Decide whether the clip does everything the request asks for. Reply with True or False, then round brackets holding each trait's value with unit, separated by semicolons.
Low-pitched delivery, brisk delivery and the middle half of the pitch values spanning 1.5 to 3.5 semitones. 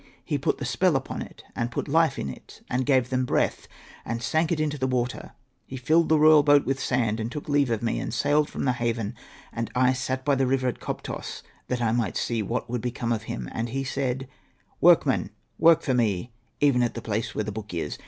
True (125 Hz; 235 wpm; 3.1 semitones)